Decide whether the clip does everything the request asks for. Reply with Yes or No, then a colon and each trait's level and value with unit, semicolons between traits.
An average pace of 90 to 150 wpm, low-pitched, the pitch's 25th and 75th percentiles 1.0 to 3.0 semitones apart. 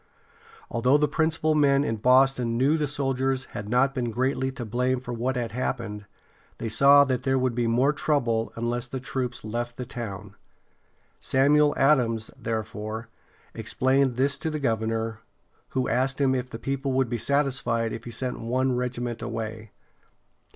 No: average, 165 wpm; low, 125 Hz; average, 2.7 semitones